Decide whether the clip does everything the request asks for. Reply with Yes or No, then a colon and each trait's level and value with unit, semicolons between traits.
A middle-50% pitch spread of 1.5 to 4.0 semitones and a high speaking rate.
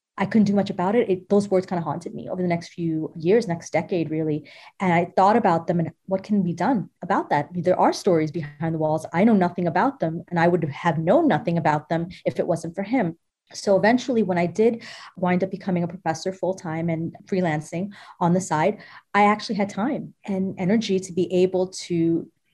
Yes: average, 2.8 semitones; fast, 230 wpm